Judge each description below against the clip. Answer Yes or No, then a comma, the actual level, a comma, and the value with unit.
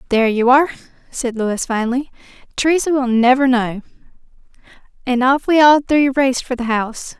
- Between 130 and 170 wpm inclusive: Yes, average, 160 wpm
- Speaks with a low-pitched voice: No, very high, 255 Hz